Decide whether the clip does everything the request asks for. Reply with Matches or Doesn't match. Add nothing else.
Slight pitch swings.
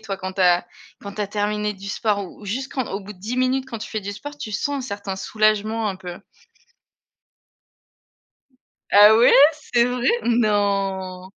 Doesn't match